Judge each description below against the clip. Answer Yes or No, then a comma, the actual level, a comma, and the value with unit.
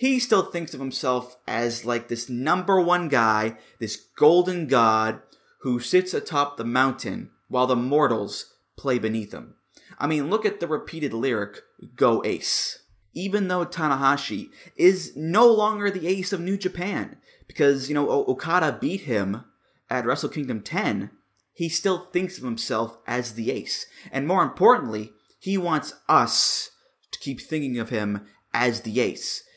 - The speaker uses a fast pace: No, average, 155 wpm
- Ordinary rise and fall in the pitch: No, wide, 7.4 semitones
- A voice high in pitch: No, low, 135 Hz